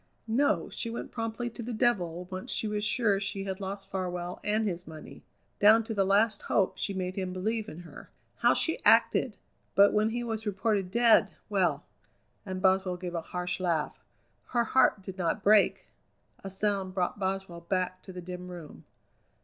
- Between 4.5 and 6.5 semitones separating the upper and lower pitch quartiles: No, average, 3.0 semitones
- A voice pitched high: Yes, high, 195 Hz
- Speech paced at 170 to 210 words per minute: Yes, average, 180 wpm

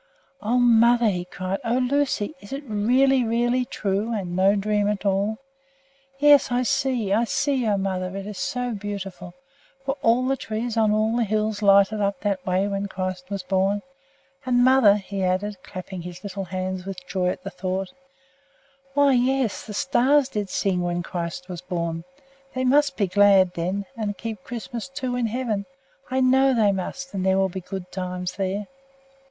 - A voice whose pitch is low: No, high, 205 Hz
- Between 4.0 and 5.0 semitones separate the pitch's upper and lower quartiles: Yes, average, 4.4 semitones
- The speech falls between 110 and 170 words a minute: No, average, 180 wpm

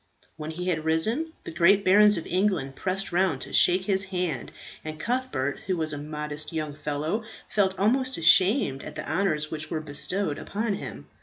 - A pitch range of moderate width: Yes, average, 4.5 semitones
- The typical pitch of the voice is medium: Yes, medium, 175 Hz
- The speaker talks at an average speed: Yes, average, 180 wpm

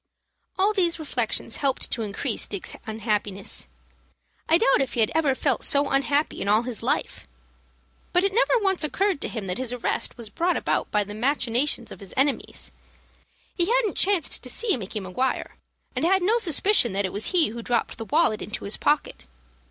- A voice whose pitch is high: Yes, very high, 265 Hz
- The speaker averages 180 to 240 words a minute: Yes, average, 190 wpm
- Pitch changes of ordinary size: No, wide, 7.8 semitones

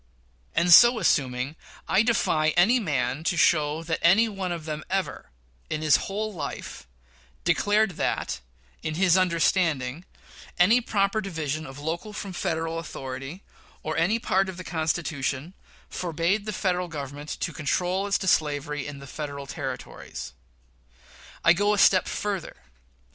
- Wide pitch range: No, average, 4.5 semitones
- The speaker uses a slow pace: No, average, 145 wpm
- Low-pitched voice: No, medium, 165 Hz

